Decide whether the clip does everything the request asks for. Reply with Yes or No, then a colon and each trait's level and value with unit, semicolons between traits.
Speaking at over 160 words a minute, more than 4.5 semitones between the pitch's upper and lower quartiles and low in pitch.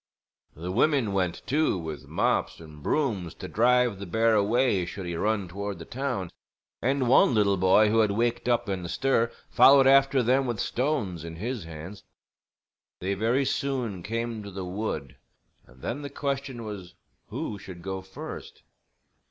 Yes: average, 170 wpm; average, 5.2 semitones; low, 105 Hz